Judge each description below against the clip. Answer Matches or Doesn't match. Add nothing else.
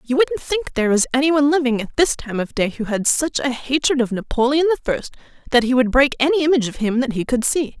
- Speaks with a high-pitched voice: Matches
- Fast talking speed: Matches